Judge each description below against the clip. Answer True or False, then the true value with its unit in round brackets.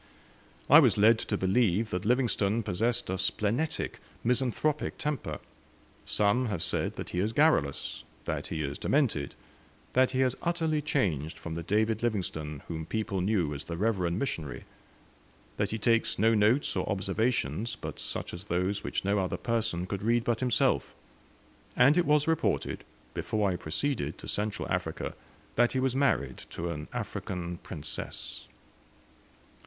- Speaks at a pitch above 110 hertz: False (105 Hz)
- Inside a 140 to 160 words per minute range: True (155 wpm)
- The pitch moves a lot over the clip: True (5.8 semitones)